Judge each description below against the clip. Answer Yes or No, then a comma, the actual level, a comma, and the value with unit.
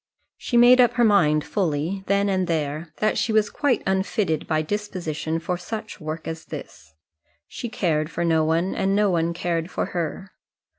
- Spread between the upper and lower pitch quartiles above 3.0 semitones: Yes, average, 4.4 semitones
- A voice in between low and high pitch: Yes, medium, 180 Hz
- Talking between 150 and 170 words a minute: No, average, 180 wpm